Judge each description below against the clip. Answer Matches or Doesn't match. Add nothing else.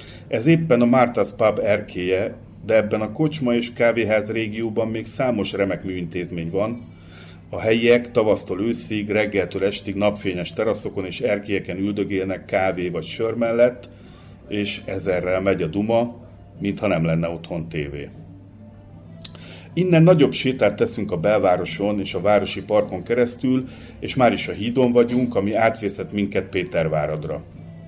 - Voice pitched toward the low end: Matches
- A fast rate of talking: Doesn't match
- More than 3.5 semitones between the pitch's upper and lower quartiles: Matches